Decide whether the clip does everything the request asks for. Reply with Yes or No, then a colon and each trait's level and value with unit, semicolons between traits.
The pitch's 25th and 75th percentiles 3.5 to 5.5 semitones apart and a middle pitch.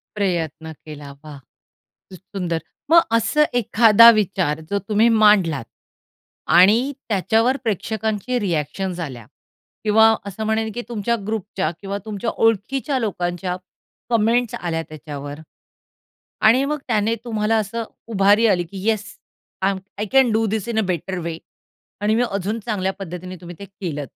No: average, 4.0 semitones; high, 205 Hz